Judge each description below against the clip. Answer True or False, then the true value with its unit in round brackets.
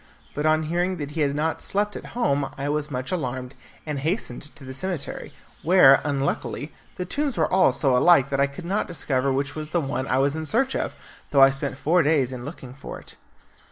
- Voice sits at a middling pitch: True (145 Hz)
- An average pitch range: True (4.1 semitones)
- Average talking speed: False (220 wpm)